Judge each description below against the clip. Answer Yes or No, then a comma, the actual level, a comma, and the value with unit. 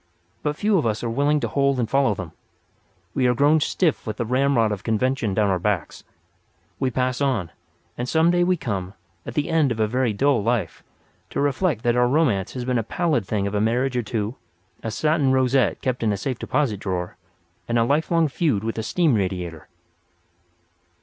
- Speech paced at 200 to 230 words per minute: Yes, fast, 205 wpm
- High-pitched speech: No, low, 125 Hz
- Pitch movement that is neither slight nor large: Yes, average, 4.8 semitones